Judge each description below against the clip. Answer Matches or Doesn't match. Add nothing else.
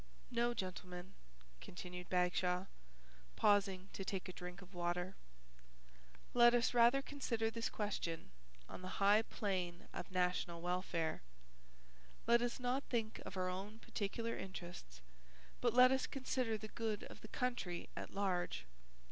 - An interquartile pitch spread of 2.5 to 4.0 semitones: Doesn't match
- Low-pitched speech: Doesn't match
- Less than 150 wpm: Matches